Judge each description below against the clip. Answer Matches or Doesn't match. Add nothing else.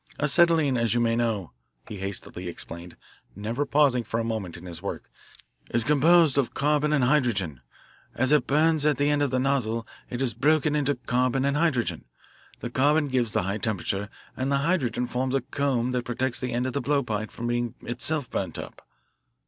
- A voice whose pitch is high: Doesn't match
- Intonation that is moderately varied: Matches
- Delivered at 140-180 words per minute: Doesn't match